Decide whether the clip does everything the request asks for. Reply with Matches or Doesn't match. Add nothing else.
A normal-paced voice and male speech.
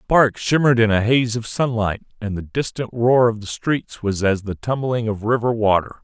Doesn't match